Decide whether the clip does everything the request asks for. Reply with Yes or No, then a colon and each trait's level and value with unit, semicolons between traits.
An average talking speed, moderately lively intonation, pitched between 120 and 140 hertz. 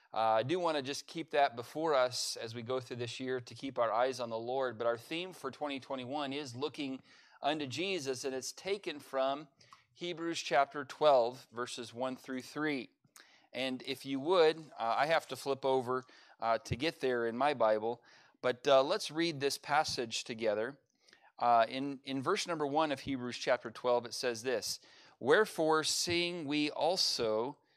Yes: average, 180 wpm; average, 3.3 semitones; low, 135 Hz